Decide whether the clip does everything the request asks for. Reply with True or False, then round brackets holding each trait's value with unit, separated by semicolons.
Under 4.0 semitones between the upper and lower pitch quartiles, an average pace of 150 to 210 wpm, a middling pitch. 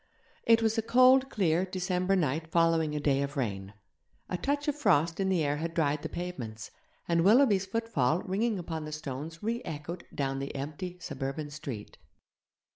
False (5.2 semitones; 175 wpm; 165 Hz)